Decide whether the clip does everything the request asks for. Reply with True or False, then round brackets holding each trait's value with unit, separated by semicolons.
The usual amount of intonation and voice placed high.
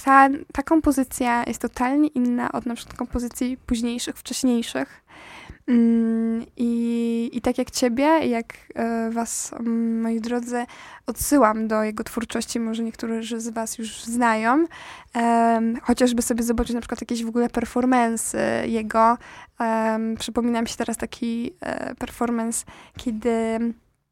False (1.3 semitones; 235 Hz)